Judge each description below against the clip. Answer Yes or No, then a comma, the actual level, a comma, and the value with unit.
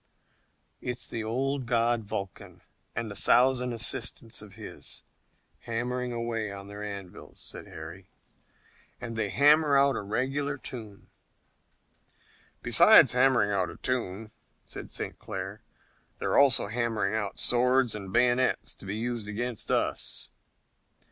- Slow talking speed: Yes, slow, 130 wpm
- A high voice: No, low, 115 Hz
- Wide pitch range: No, average, 3.4 semitones